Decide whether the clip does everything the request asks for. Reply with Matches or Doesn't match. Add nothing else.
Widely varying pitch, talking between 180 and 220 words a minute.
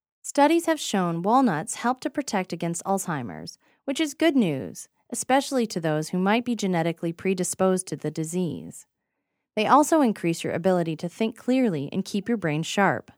Doesn't match